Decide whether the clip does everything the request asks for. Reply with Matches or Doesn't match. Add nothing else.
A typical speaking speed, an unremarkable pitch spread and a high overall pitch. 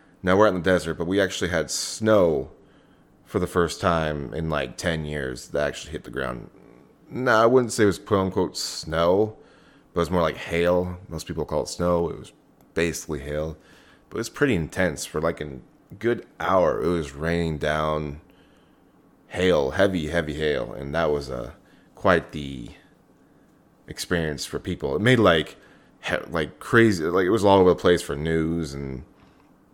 Doesn't match